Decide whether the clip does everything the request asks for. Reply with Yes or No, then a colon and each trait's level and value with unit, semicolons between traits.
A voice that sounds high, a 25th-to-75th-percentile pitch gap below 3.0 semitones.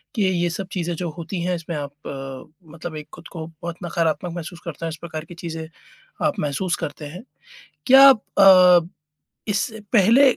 No: medium, 170 Hz; narrow, 2.6 semitones